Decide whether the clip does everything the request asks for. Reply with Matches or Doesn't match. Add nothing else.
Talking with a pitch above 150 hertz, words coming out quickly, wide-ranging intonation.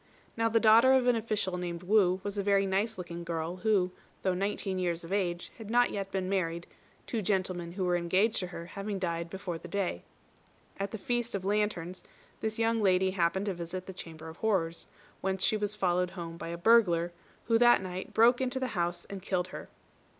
Doesn't match